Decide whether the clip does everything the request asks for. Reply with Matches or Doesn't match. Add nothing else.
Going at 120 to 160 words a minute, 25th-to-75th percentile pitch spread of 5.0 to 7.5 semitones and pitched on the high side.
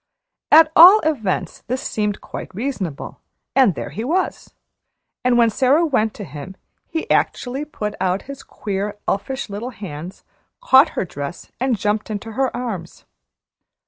Matches